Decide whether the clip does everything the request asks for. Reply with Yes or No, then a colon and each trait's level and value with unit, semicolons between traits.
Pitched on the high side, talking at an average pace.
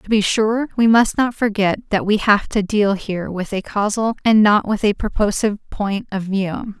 No: high, 210 Hz; fast, 210 wpm